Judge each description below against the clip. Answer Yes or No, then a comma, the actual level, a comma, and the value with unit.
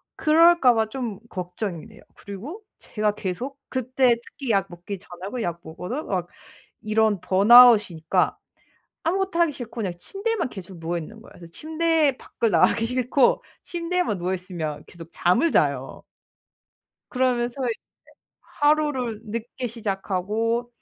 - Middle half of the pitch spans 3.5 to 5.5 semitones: No, wide, 6.2 semitones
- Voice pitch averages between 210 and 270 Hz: Yes, high, 225 Hz